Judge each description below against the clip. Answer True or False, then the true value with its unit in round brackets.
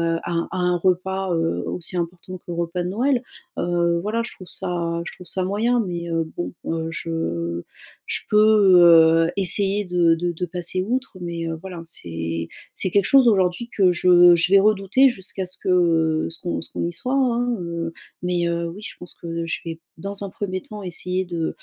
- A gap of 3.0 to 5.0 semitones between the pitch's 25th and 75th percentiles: False (2.6 semitones)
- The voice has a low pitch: False (180 Hz)